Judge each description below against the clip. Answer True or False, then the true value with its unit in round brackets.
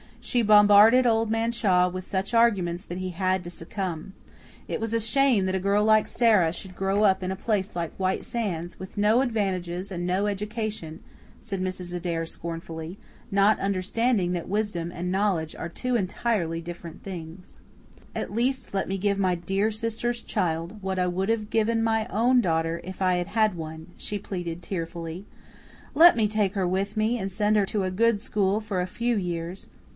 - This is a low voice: False (195 Hz)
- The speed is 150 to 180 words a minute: False (190 wpm)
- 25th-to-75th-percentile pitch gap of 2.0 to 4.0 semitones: True (3.4 semitones)